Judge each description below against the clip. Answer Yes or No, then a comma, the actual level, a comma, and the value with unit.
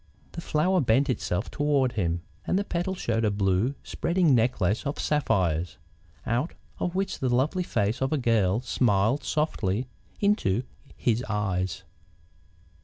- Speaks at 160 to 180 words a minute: No, average, 140 wpm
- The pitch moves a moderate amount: No, wide, 6.9 semitones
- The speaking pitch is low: Yes, low, 120 Hz